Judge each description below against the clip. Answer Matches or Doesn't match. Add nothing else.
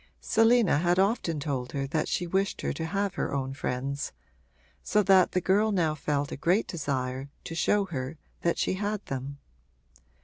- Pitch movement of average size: Doesn't match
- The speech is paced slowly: Doesn't match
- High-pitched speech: Doesn't match